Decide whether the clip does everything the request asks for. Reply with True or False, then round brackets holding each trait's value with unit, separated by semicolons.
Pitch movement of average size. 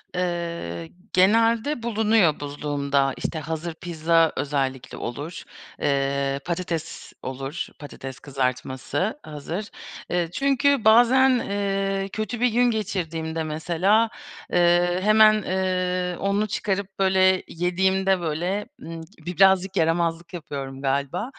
True (4.4 semitones)